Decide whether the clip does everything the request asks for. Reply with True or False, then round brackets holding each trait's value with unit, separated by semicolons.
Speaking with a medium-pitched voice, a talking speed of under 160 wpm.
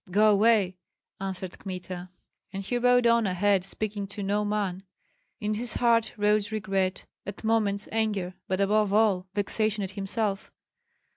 False (205 Hz; 145 wpm)